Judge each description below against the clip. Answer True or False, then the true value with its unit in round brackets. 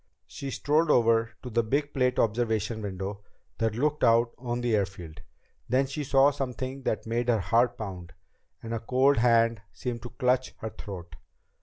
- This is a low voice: True (115 Hz)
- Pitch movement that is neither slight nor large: True (3.0 semitones)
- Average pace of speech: True (175 wpm)